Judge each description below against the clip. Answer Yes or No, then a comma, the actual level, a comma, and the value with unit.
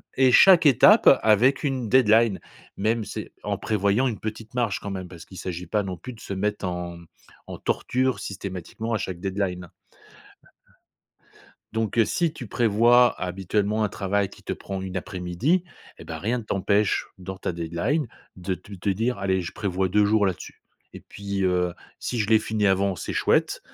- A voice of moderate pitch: No, low, 100 Hz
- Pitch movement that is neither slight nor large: Yes, average, 3.6 semitones